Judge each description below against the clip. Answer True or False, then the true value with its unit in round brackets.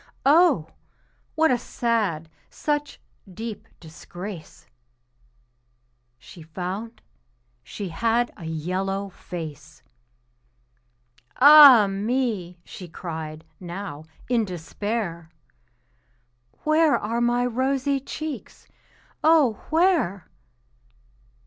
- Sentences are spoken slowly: True (80 wpm)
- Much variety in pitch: True (6.9 semitones)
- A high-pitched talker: True (210 Hz)